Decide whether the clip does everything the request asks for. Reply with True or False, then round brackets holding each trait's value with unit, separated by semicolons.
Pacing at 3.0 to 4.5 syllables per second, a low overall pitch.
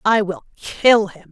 False (3.6 syllables/s; 195 Hz)